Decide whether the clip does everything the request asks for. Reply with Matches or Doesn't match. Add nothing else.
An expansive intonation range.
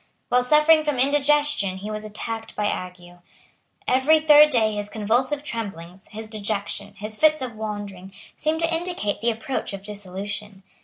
Matches